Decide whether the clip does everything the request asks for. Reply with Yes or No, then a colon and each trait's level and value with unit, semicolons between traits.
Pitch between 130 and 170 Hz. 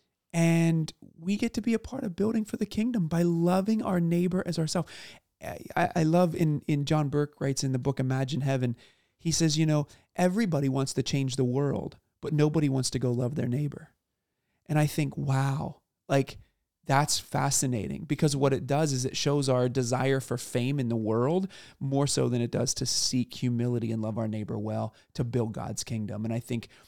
Yes: medium, 140 Hz